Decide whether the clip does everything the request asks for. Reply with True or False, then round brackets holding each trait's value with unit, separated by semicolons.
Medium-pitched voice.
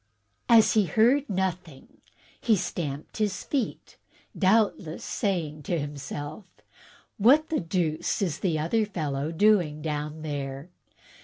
True (170 Hz)